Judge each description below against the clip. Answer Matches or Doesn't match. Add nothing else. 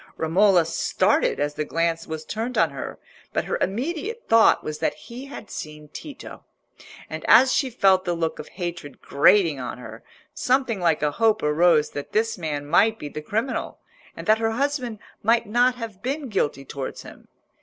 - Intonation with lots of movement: Matches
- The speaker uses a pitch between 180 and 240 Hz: Matches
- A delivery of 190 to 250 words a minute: Doesn't match